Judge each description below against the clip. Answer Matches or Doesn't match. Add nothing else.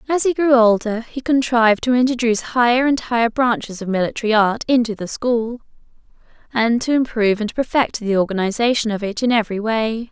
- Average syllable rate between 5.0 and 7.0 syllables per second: Matches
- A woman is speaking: Matches